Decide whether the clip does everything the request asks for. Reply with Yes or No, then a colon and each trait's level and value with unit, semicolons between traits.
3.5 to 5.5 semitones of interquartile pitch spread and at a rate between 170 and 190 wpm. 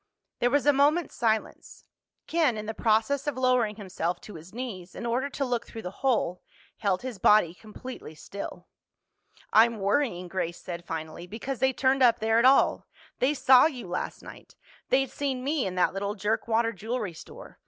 Yes: average, 5.1 semitones; average, 180 wpm